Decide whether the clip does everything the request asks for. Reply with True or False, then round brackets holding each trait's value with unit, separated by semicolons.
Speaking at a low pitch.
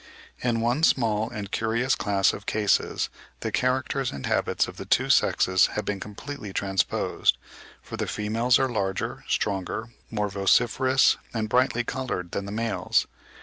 True (110 Hz)